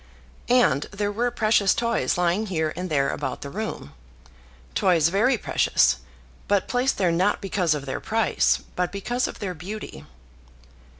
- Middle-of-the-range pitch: No, high, 195 Hz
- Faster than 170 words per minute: No, average, 155 wpm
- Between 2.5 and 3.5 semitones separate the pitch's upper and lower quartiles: No, average, 5.0 semitones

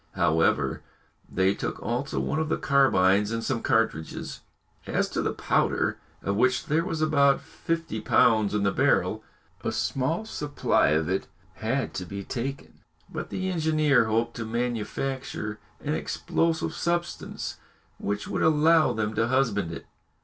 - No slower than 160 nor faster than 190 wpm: No, average, 150 wpm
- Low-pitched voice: Yes, low, 120 Hz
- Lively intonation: Yes, wide, 6.4 semitones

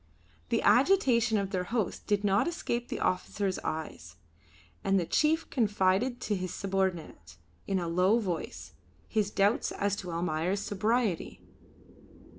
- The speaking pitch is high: Yes, high, 195 Hz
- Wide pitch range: No, average, 3.6 semitones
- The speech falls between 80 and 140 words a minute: Yes, slow, 135 wpm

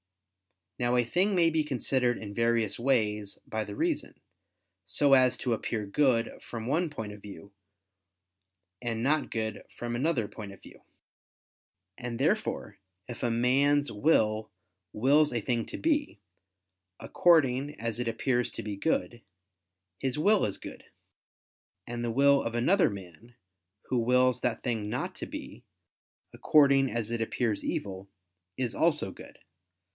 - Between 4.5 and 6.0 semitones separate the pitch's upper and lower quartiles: No, average, 4.1 semitones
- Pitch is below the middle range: Yes, low, 120 Hz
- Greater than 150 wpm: No, average, 145 wpm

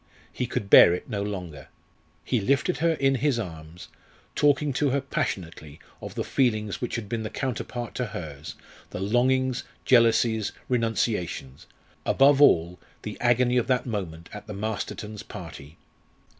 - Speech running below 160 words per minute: Yes, average, 150 wpm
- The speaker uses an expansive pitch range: Yes, wide, 5.8 semitones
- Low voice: Yes, low, 110 Hz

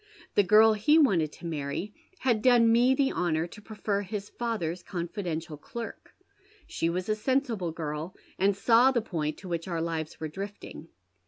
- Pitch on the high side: Yes, high, 195 Hz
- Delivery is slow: No, average, 170 wpm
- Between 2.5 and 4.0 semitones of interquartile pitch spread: No, wide, 5.4 semitones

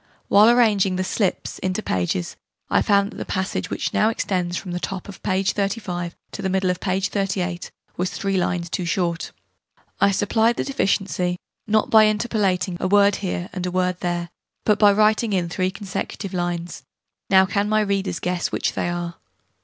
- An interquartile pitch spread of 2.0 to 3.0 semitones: Yes, narrow, 2.4 semitones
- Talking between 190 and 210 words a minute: No, average, 180 wpm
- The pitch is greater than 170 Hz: Yes, high, 190 Hz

